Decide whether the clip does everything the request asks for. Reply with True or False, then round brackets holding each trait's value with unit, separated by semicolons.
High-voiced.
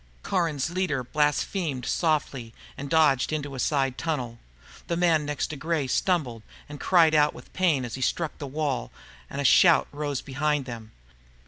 False (150 Hz)